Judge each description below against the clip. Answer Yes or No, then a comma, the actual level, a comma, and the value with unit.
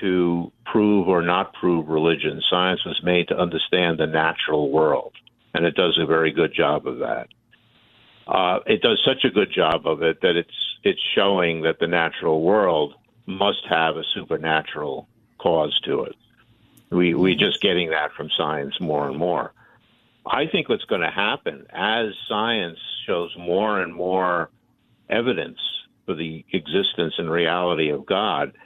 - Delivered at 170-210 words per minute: No, average, 160 wpm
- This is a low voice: Yes, very low, 85 Hz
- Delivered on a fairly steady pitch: Yes, narrow, 1.6 semitones